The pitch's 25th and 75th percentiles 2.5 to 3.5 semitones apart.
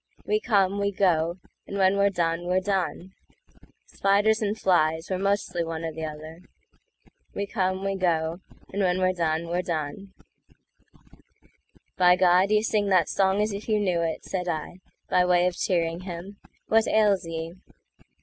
Yes: average, 2.9 semitones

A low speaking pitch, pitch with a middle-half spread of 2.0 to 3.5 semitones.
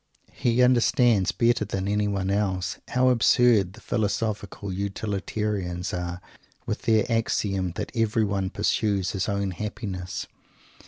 Yes: low, 100 Hz; average, 2.9 semitones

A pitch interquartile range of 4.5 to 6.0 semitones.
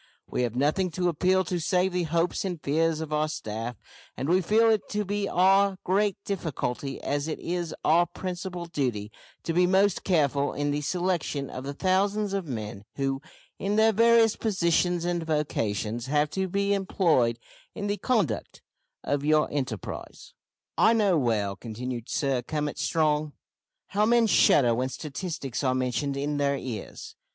Yes: wide, 5.6 semitones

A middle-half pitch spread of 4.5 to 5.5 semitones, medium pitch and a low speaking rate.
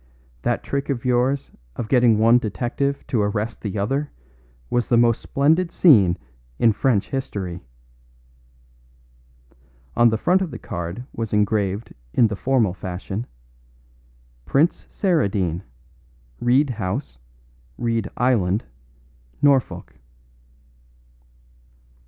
No: average, 4.8 semitones; low, 115 Hz; slow, 105 wpm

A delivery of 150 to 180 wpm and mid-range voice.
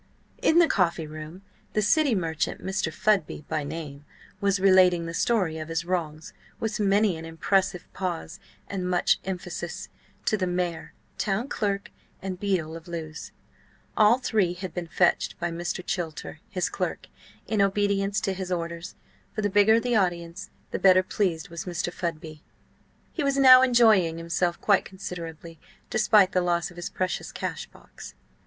Yes: average, 160 wpm; medium, 180 Hz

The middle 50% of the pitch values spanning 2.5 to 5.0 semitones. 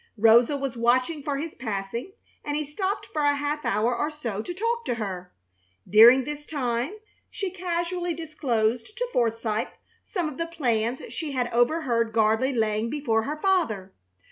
No: wide, 5.5 semitones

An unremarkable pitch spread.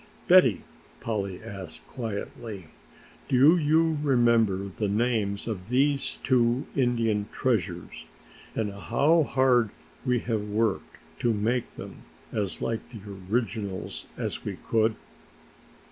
Yes: average, 3.6 semitones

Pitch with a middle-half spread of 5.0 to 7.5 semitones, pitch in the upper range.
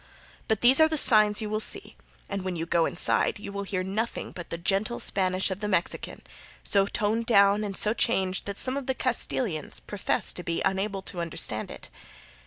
No: average, 2.9 semitones; high, 200 Hz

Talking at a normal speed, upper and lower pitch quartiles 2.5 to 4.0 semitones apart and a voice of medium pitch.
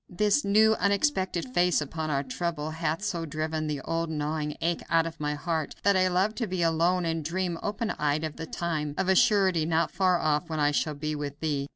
No: fast, 220 wpm; average, 3.3 semitones; medium, 165 Hz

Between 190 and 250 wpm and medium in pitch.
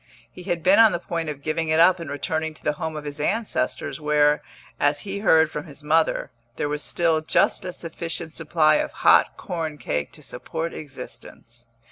Yes: average, 195 wpm; medium, 160 Hz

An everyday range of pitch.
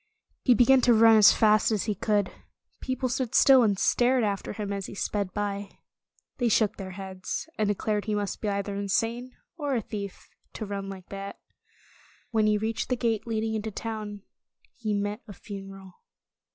No: narrow, 2.2 semitones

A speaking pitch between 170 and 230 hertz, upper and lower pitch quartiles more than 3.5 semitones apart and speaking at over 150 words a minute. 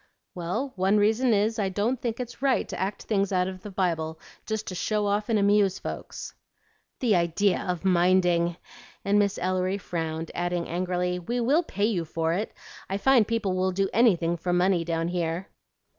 No: high, 190 Hz; average, 3.1 semitones; average, 185 wpm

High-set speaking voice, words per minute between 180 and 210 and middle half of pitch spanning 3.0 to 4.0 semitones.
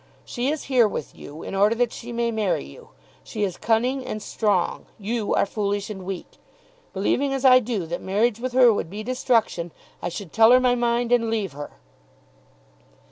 Yes: high, 225 Hz; average, 190 wpm; average, 3.6 semitones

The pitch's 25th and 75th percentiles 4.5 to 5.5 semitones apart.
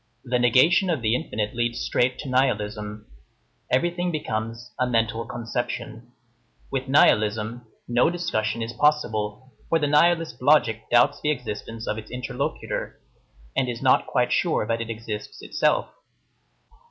No: average, 3.2 semitones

